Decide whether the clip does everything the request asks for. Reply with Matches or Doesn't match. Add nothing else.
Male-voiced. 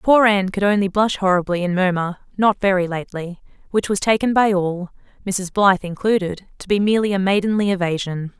Doesn't match